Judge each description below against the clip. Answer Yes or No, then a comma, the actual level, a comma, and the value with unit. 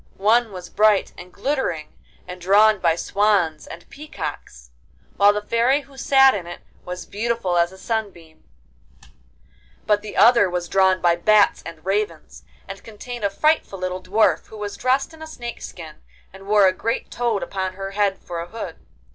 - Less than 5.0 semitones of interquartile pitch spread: Yes, average, 4.1 semitones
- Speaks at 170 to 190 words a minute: Yes, average, 175 wpm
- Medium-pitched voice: No, high, 200 Hz